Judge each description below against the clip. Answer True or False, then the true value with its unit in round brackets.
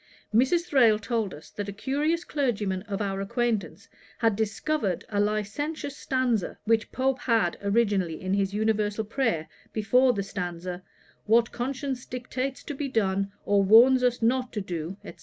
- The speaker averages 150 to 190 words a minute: True (160 wpm)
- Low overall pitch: False (220 Hz)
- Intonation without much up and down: False (4.4 semitones)